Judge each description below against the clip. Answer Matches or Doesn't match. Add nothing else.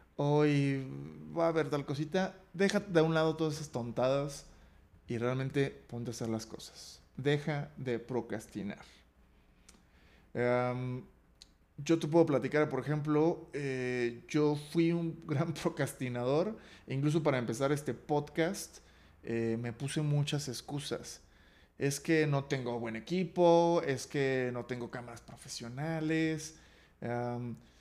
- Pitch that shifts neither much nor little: Matches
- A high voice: Doesn't match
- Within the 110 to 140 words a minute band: Matches